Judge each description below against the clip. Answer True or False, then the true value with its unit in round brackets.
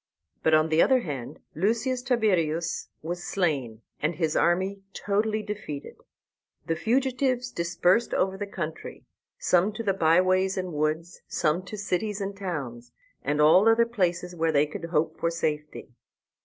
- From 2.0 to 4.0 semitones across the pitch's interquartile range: False (4.6 semitones)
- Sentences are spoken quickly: False (155 wpm)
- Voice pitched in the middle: True (180 Hz)